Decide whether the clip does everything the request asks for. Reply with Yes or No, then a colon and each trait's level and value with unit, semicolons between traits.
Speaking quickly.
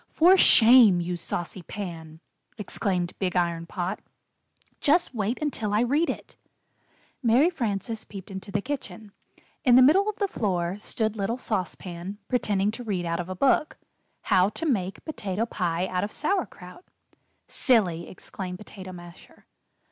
No: average, 155 wpm